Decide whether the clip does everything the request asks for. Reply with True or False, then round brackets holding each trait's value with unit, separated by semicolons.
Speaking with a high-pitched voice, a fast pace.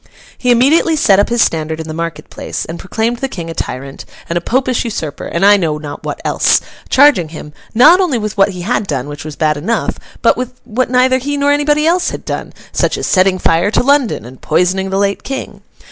True (200 Hz; 225 wpm)